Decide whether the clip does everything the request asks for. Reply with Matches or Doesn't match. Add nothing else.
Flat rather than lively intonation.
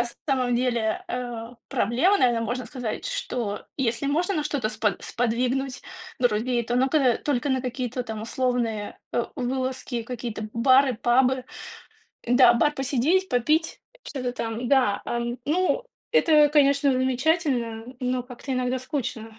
Matches